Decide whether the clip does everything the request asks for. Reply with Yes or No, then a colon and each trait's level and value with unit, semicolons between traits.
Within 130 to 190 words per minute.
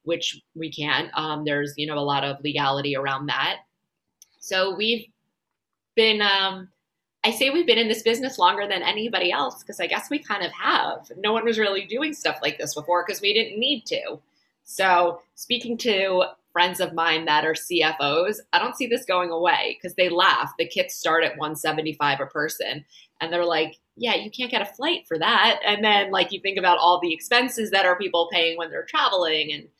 No: fast, 205 wpm